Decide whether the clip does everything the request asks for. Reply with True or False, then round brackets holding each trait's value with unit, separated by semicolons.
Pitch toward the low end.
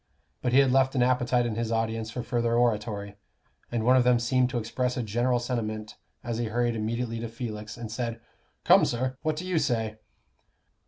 True (120 Hz)